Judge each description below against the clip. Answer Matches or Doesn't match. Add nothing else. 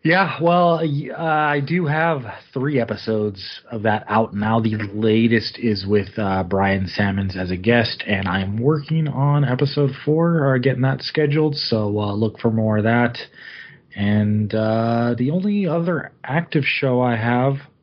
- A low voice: Matches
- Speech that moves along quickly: Doesn't match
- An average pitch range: Doesn't match